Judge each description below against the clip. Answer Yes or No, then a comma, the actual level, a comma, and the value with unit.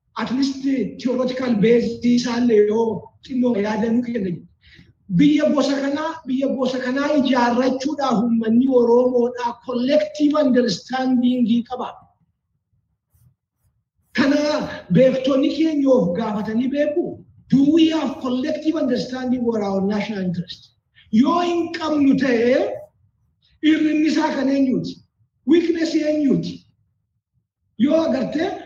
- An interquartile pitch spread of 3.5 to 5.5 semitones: Yes, average, 4.1 semitones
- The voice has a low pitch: No, very high, 255 Hz